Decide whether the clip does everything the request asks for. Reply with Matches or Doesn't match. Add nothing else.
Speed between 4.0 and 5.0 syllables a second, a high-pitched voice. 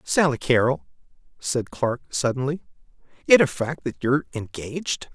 Doesn't match